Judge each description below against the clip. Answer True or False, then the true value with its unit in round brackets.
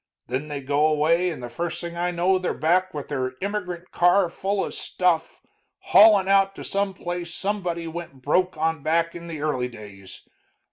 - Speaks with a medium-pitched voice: True (170 Hz)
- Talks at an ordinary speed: True (185 wpm)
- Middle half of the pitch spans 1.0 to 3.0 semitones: False (3.5 semitones)